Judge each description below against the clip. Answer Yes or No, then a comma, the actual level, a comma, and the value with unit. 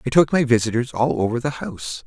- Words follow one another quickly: Yes, fast, 230 wpm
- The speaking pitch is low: Yes, low, 120 Hz